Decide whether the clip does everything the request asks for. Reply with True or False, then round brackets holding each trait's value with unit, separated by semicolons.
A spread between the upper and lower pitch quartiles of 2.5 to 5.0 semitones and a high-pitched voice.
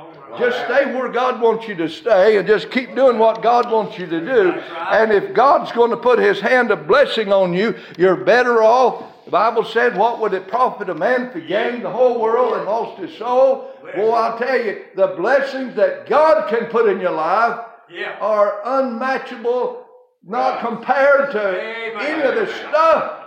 True (3.7 semitones; 235 Hz)